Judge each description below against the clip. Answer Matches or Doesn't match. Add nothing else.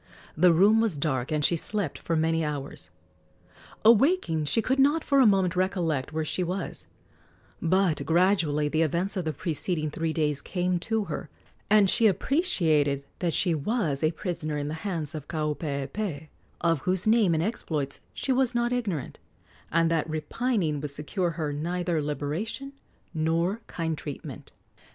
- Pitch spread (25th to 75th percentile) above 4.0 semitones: Matches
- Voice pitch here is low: Doesn't match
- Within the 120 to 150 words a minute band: Doesn't match